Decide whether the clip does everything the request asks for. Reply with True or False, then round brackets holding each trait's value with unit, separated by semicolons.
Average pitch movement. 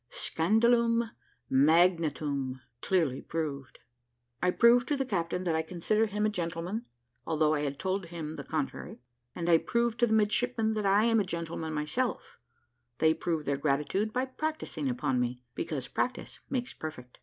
False (6.4 semitones)